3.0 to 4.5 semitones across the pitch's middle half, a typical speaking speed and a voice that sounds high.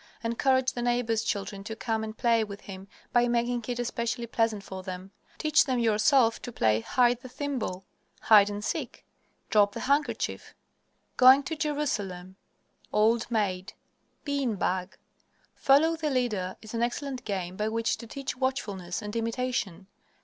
Yes: average, 3.9 semitones; average, 155 wpm; high, 230 Hz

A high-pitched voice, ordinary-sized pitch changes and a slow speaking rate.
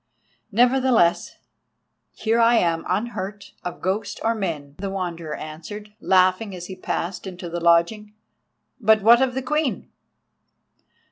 Yes: high, 195 Hz; average, 4.6 semitones; slow, 130 wpm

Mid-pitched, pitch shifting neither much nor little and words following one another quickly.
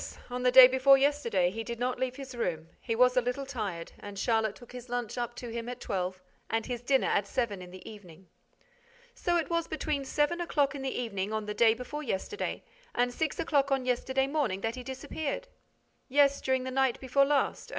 No: very high, 250 Hz; average, 3.6 semitones; fast, 210 wpm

